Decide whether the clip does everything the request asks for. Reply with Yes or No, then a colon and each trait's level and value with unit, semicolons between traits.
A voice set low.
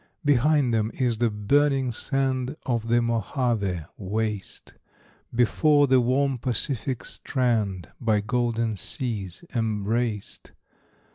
Yes: low, 120 Hz